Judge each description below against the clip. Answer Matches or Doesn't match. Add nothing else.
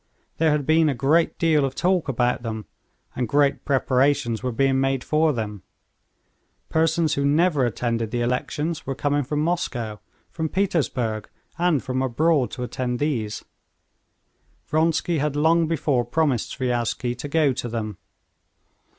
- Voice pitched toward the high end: Doesn't match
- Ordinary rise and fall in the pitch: Matches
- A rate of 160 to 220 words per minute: Doesn't match